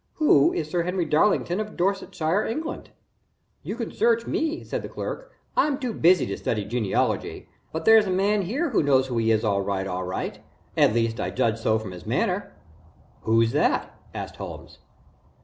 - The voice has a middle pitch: Yes, medium, 165 Hz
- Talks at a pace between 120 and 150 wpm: No, average, 185 wpm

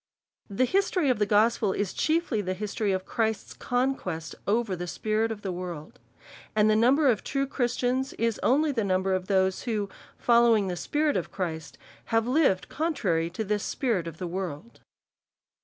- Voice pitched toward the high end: Yes, high, 215 Hz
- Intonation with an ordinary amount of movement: Yes, average, 4.9 semitones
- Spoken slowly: No, average, 175 wpm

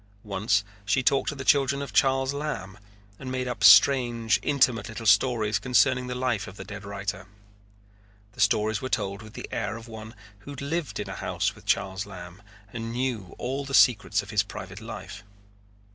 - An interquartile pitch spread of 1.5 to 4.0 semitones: No, average, 4.4 semitones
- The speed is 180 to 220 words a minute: Yes, average, 190 wpm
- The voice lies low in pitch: Yes, low, 115 Hz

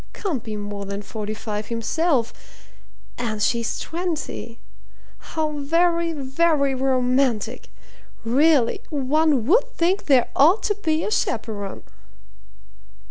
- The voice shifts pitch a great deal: Yes, wide, 6.0 semitones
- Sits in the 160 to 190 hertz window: No, very high, 270 Hz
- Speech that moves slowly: Yes, slow, 110 wpm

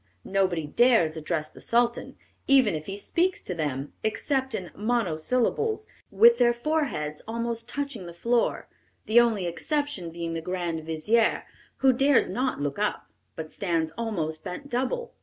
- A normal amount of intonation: No, wide, 6.8 semitones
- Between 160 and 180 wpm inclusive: No, average, 150 wpm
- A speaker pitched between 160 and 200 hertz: No, high, 215 Hz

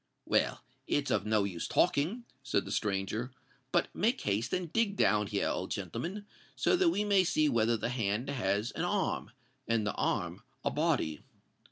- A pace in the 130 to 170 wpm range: Yes, average, 165 wpm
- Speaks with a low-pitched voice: Yes, low, 125 Hz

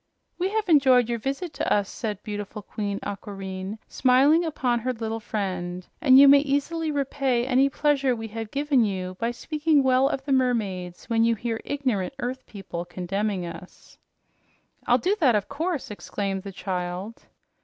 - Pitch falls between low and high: No, high, 235 Hz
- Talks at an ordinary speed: Yes, average, 165 wpm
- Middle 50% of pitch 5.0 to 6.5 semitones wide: Yes, wide, 5.6 semitones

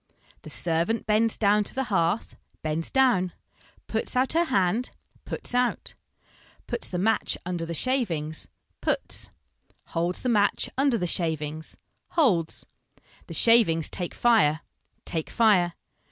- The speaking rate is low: Yes, slow, 130 wpm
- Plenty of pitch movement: Yes, wide, 6.1 semitones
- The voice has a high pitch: Yes, high, 195 Hz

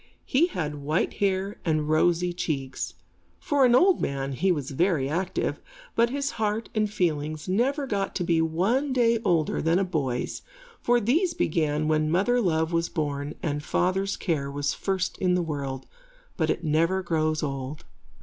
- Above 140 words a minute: Yes, average, 170 wpm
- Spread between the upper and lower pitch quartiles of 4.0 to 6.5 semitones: Yes, average, 5.0 semitones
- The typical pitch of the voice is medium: Yes, medium, 170 Hz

